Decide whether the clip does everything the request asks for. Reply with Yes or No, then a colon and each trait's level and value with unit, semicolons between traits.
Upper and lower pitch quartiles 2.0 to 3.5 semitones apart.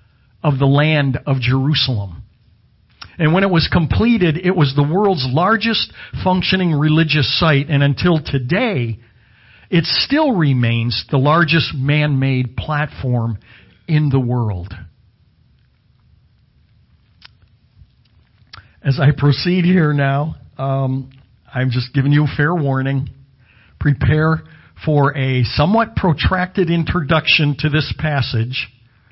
No: average, 4.5 semitones